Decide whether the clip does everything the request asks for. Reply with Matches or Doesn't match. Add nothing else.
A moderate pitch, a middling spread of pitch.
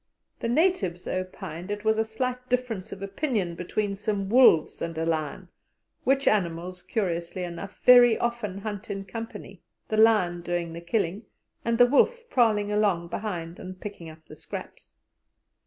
Doesn't match